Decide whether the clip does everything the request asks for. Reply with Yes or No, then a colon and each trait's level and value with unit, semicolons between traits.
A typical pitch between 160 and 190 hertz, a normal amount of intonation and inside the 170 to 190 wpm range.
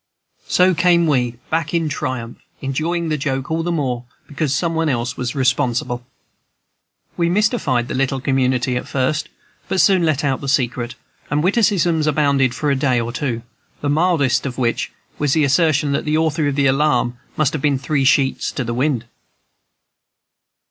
No: medium, 140 Hz; average, 3.6 semitones; average, 175 wpm